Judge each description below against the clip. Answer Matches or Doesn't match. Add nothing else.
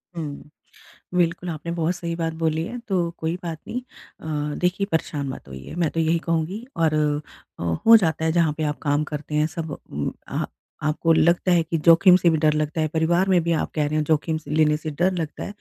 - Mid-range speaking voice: Matches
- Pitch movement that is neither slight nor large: Doesn't match